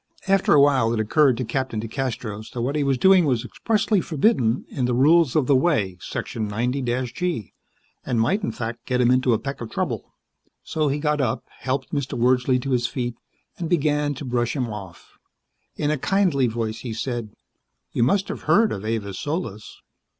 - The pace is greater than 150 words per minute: Yes, average, 190 wpm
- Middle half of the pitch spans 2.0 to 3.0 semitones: No, average, 4.3 semitones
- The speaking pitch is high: No, low, 130 Hz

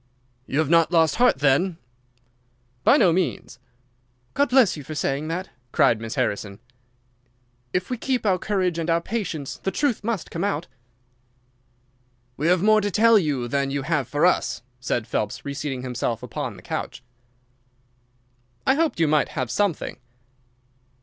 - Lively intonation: Yes, wide, 6.7 semitones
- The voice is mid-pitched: Yes, medium, 165 Hz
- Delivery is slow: No, average, 155 wpm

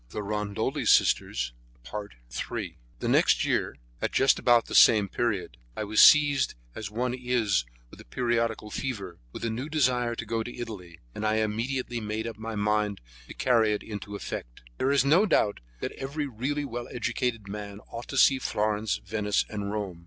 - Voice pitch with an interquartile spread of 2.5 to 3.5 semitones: Yes, average, 3.1 semitones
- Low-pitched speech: Yes, low, 110 Hz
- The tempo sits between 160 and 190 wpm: Yes, average, 170 wpm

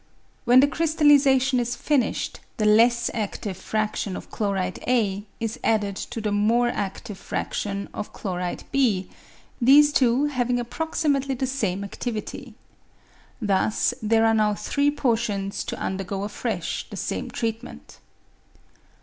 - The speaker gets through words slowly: Yes, slow, 130 wpm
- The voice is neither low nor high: No, high, 225 Hz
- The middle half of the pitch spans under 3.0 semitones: No, average, 4.1 semitones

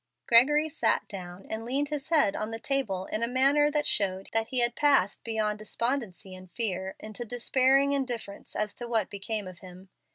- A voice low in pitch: No, high, 230 Hz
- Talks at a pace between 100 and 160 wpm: No, average, 185 wpm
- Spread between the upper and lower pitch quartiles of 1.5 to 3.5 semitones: No, wide, 5.4 semitones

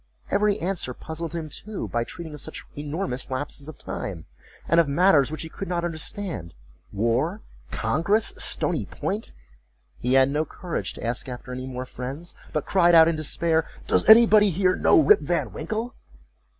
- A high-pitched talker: No, medium, 160 Hz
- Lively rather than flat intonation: Yes, wide, 6.3 semitones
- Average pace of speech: Yes, average, 160 wpm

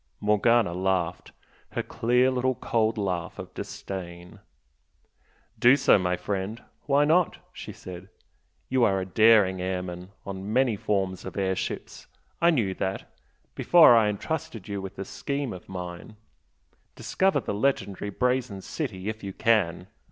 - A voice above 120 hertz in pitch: No, low, 100 Hz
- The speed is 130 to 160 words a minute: Yes, average, 140 wpm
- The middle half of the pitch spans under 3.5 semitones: No, average, 4.3 semitones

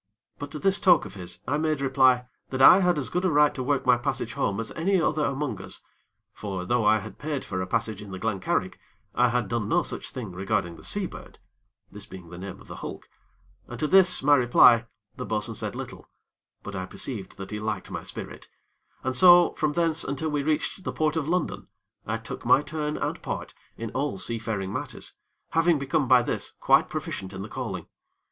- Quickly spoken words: Yes, fast, 215 wpm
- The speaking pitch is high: No, low, 125 Hz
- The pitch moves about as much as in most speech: No, wide, 6.3 semitones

